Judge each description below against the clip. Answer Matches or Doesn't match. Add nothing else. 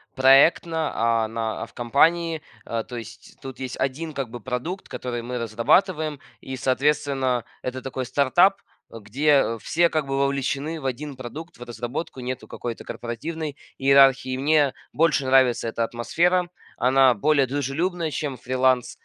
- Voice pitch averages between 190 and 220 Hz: Doesn't match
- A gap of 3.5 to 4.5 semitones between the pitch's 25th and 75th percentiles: Matches